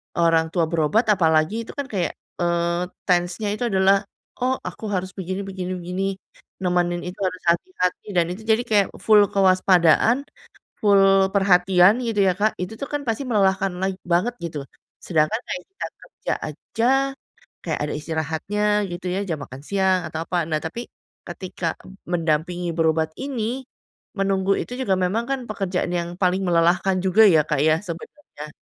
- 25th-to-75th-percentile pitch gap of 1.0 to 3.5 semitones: Yes, average, 3.0 semitones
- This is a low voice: No, medium, 185 Hz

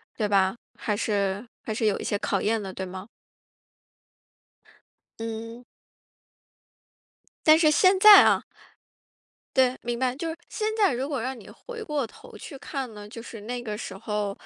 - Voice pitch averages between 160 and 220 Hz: No, high, 230 Hz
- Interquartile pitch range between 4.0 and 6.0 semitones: Yes, average, 4.9 semitones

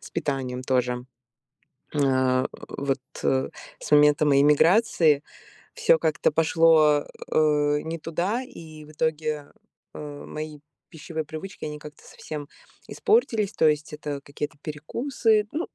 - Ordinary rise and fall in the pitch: No, narrow, 1.9 semitones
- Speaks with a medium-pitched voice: Yes, medium, 150 Hz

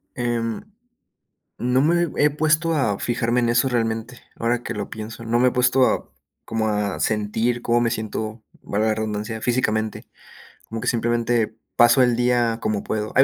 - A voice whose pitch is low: Yes, low, 115 Hz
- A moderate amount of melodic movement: No, narrow, 1.9 semitones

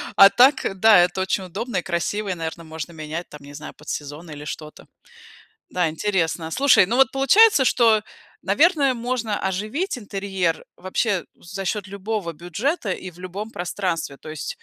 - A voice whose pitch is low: No, high, 190 Hz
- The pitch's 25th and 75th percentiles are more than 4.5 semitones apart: Yes, average, 5.1 semitones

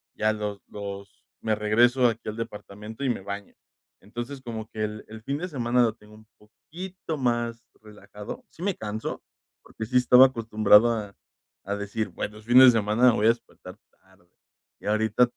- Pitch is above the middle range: No, low, 110 Hz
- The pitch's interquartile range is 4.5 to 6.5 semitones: No, narrow, 2.5 semitones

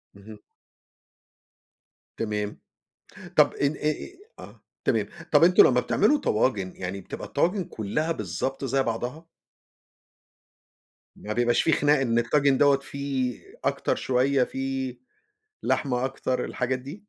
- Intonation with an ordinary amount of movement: Yes, average, 3.5 semitones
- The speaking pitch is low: Yes, low, 130 Hz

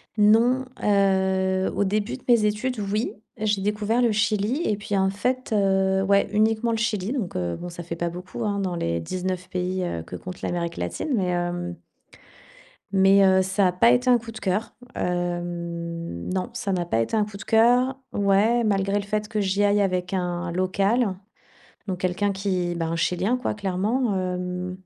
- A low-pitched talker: No, high, 195 Hz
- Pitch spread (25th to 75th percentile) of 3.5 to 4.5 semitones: No, average, 2.9 semitones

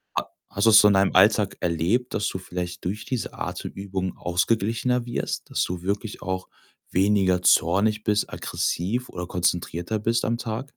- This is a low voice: Yes, low, 100 Hz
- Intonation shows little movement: No, average, 3.5 semitones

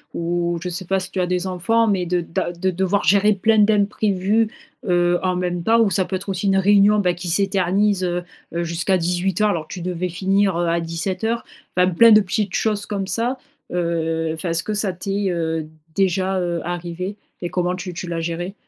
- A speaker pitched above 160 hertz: Yes, medium, 185 Hz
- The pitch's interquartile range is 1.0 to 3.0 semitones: Yes, narrow, 2.5 semitones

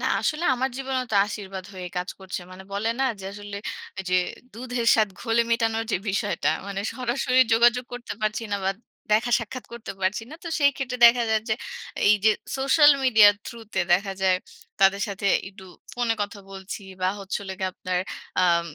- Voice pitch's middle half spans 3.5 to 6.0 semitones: Yes, average, 3.9 semitones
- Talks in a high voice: Yes, high, 215 Hz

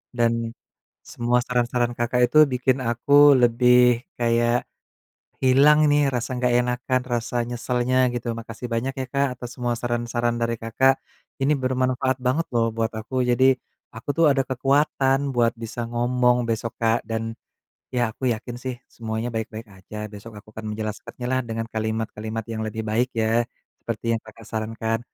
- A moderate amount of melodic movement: No, narrow, 2.1 semitones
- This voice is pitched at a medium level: No, low, 120 Hz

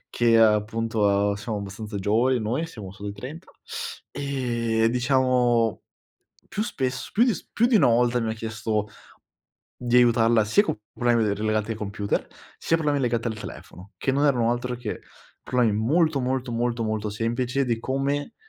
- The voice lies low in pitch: Yes, low, 115 Hz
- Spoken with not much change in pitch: No, average, 3.0 semitones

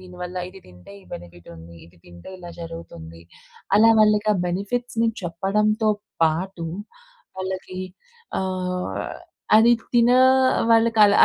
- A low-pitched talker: No, medium, 185 Hz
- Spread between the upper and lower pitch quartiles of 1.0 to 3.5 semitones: No, average, 4.8 semitones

